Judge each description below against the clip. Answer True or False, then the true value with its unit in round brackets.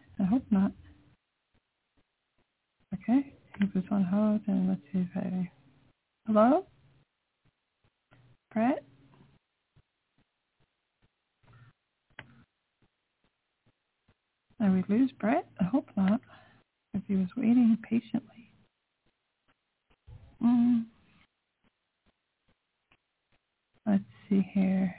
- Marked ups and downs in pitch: False (3.6 semitones)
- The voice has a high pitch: True (210 Hz)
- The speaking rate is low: True (70 wpm)